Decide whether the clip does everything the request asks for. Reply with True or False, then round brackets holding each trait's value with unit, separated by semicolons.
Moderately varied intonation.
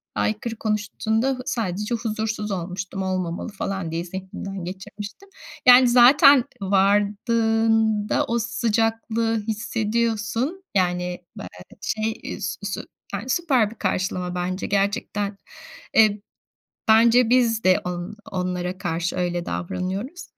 True (3.4 semitones)